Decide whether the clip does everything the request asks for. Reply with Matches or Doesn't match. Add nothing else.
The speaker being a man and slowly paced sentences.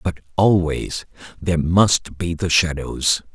Matches